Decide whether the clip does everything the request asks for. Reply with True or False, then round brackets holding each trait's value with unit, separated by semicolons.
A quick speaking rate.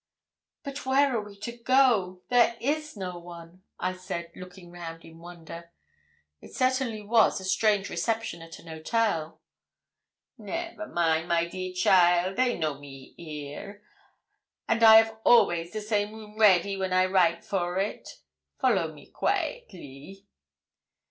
False (140 wpm)